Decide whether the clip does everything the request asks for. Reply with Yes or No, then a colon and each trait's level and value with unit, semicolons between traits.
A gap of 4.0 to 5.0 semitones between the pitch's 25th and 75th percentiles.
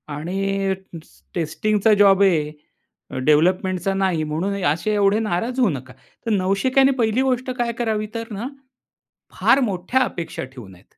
Yes: average, 4.7 semitones